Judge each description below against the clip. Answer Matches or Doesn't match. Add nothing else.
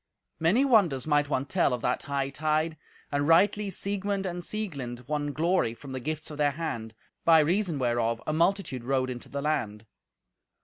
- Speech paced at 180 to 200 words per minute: Doesn't match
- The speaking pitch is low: Doesn't match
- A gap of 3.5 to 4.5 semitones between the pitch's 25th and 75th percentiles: Doesn't match